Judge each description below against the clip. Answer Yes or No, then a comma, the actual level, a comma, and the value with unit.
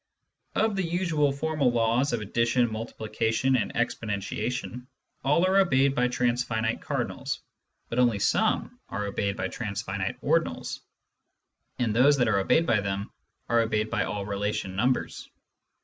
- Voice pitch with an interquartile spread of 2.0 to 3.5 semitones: No, average, 3.9 semitones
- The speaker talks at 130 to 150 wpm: Yes, average, 145 wpm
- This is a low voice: Yes, low, 115 Hz